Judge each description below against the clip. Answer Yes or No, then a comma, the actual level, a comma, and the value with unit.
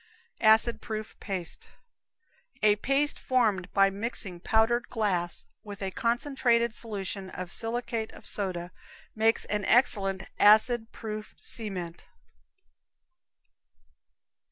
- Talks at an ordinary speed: No, slow, 100 wpm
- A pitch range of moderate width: Yes, average, 3.2 semitones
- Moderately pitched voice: No, high, 215 Hz